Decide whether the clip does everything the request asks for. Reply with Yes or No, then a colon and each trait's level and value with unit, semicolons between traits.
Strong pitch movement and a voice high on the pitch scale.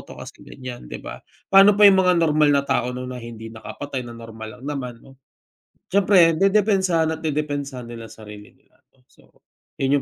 No: wide, 5.8 semitones; medium, 140 Hz